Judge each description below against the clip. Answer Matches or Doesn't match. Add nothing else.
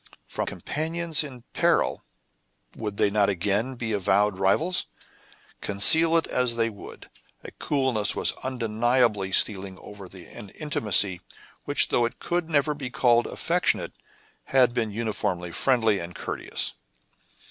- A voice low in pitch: Matches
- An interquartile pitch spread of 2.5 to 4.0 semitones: Doesn't match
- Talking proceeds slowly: Matches